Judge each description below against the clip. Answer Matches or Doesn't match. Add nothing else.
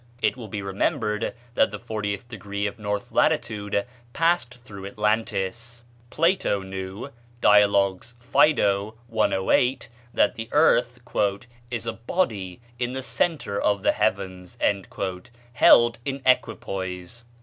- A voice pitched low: Matches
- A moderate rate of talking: Doesn't match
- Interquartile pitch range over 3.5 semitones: Doesn't match